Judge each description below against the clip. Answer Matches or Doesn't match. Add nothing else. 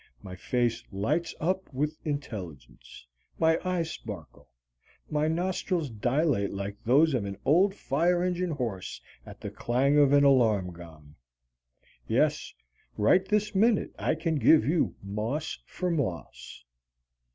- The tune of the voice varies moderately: Doesn't match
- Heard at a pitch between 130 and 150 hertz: Matches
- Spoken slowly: Matches